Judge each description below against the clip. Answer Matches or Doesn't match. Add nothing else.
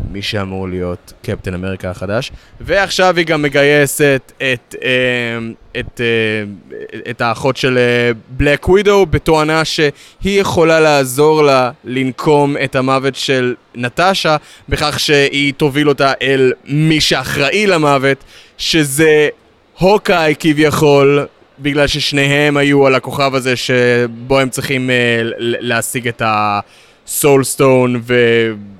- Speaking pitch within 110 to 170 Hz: Matches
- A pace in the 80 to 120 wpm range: Matches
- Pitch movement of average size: Matches